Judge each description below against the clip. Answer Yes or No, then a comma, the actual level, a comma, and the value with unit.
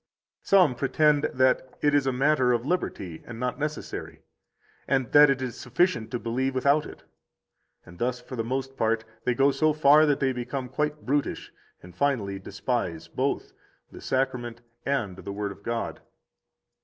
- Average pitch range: Yes, average, 3.4 semitones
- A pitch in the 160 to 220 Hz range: No, low, 130 Hz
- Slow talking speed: No, average, 165 wpm